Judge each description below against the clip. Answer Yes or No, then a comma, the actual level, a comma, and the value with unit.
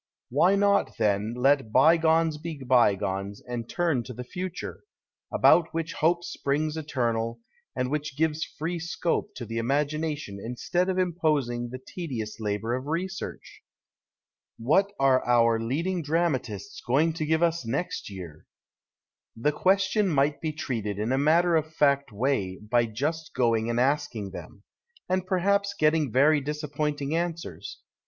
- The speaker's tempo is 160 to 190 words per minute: No, average, 145 wpm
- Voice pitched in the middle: Yes, medium, 145 Hz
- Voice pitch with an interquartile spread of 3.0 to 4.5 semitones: No, wide, 5.6 semitones